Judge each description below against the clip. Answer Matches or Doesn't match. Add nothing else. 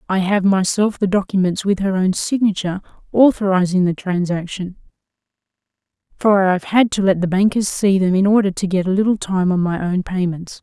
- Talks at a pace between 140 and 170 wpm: Doesn't match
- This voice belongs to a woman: Matches